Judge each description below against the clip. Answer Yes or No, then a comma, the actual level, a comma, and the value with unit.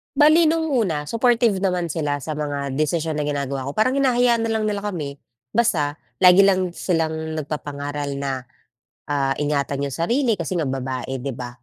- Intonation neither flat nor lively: No, wide, 6.8 semitones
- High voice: No, medium, 160 Hz